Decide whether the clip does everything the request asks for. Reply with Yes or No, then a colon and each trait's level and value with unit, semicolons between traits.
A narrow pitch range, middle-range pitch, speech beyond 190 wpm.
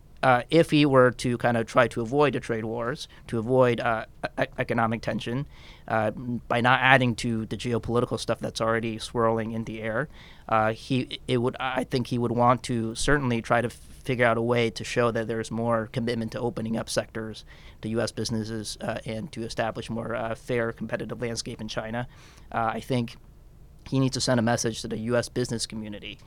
No: narrow, 1.7 semitones; low, 115 Hz; fast, 205 wpm